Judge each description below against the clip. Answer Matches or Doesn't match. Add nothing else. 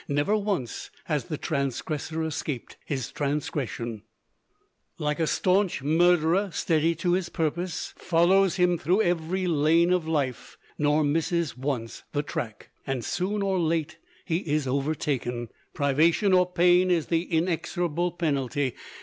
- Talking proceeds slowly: Matches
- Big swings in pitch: Doesn't match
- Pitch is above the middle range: Doesn't match